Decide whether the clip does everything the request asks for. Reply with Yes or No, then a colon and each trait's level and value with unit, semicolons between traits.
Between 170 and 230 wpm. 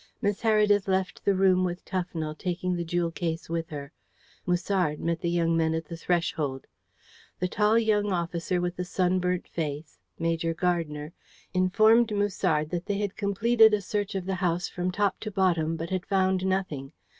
Yes: average, 175 wpm